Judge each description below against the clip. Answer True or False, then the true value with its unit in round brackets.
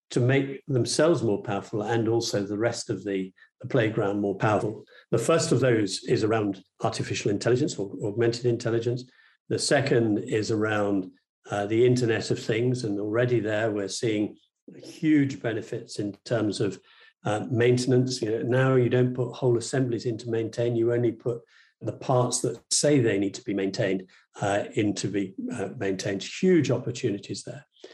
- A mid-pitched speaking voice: False (115 Hz)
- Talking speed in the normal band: True (170 wpm)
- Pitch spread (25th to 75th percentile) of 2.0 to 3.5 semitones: True (3.2 semitones)